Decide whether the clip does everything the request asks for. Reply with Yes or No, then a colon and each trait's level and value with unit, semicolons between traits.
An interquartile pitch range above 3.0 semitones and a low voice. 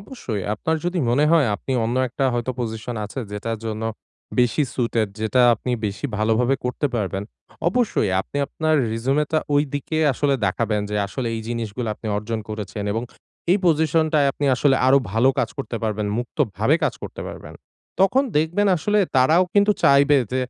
Yes: average, 5.3 semitones; low, 125 Hz